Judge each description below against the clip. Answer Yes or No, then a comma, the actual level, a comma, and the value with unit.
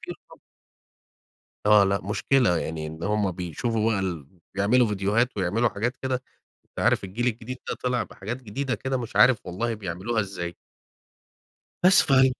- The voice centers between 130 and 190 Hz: No, low, 110 Hz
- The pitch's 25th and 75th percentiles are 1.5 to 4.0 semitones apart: No, average, 4.4 semitones